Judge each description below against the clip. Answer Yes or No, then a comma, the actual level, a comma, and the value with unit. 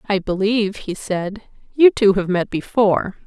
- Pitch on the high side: Yes, high, 205 Hz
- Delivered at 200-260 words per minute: No, average, 165 wpm